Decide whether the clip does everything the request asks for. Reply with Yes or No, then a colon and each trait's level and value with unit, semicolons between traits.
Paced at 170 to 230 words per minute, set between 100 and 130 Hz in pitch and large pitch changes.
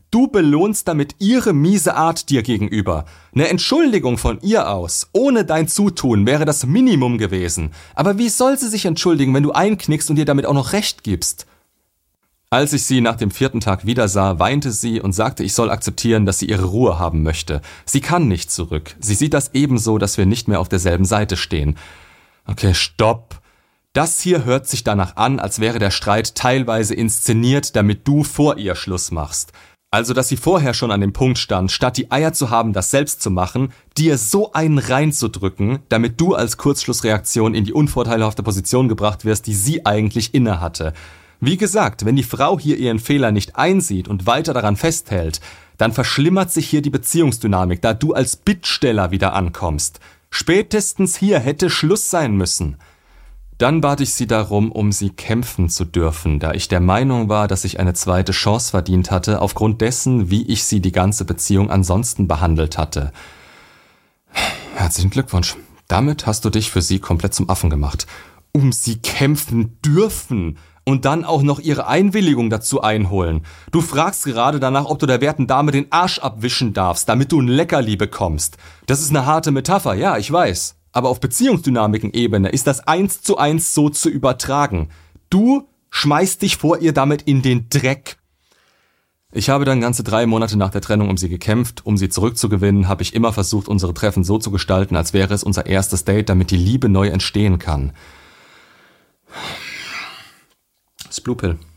Yes: average, 180 wpm; low, 115 Hz; wide, 7.0 semitones